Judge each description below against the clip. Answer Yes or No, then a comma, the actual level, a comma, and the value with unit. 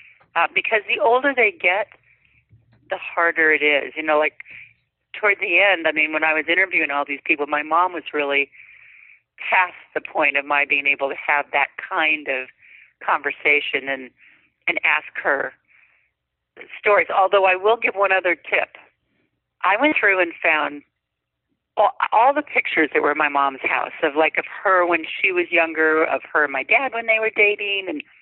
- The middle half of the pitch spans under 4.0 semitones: No, average, 4.9 semitones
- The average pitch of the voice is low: No, medium, 160 Hz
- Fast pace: No, average, 185 wpm